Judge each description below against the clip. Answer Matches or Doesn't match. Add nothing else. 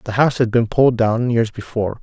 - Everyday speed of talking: Doesn't match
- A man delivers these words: Matches